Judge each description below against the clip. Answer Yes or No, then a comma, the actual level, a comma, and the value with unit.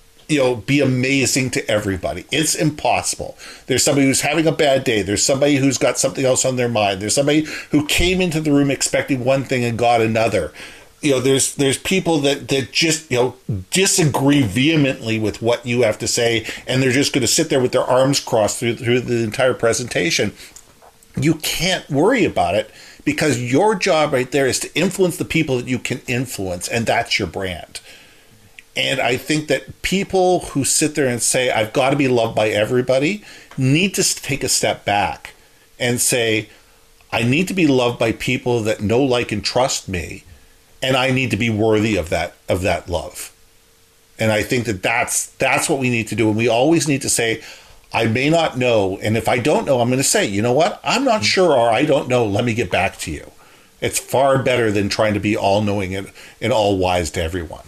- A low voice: Yes, low, 125 Hz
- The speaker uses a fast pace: Yes, fast, 210 wpm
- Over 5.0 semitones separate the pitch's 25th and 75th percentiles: No, average, 4.0 semitones